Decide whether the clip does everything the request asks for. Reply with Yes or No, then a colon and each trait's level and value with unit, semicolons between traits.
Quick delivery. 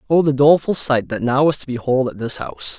Yes: fast, 260 wpm